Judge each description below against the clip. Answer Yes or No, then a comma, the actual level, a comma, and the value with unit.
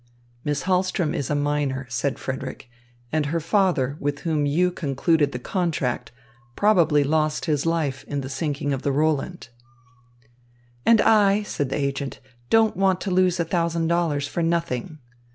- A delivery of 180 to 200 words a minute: No, average, 155 wpm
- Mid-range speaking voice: Yes, medium, 155 Hz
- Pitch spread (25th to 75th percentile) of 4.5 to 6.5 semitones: No, average, 3.7 semitones